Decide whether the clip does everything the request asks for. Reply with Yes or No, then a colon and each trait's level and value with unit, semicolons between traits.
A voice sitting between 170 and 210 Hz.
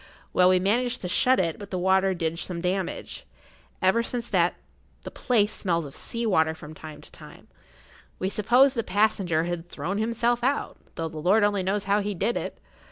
Yes: high, 190 Hz